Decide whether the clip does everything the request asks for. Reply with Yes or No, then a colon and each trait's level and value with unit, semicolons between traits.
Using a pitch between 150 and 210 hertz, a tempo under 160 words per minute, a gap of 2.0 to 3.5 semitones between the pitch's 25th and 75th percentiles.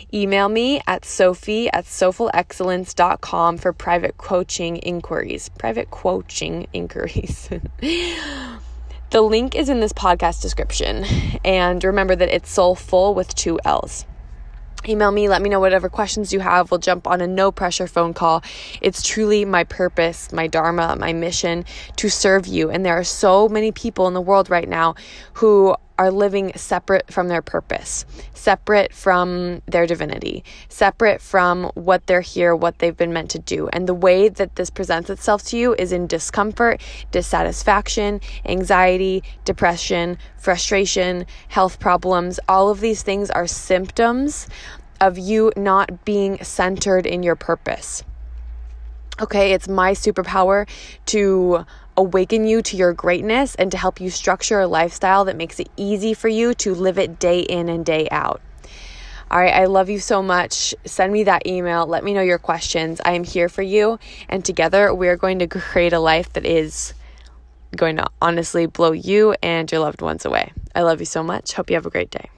No: medium, 185 Hz; average, 170 wpm; narrow, 2.5 semitones